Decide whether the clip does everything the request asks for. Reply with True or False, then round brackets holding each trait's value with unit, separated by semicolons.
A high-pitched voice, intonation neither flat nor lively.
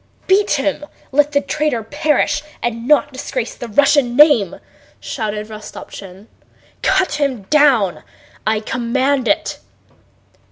True (265 Hz; 4.8 semitones)